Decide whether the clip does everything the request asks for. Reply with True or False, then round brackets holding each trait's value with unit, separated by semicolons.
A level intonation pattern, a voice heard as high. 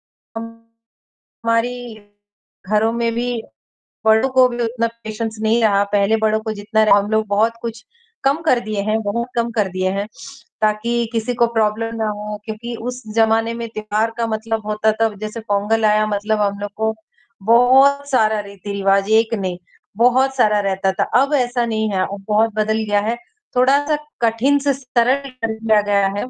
True (1.9 semitones; 220 Hz)